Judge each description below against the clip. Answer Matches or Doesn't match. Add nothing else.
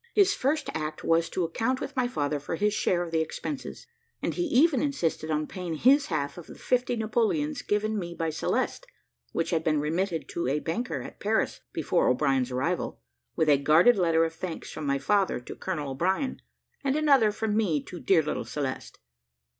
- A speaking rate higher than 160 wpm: Matches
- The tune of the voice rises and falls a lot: Matches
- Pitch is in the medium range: Matches